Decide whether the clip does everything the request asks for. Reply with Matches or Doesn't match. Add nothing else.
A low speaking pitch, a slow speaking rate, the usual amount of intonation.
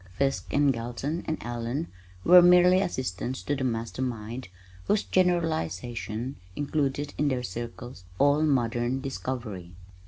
Matches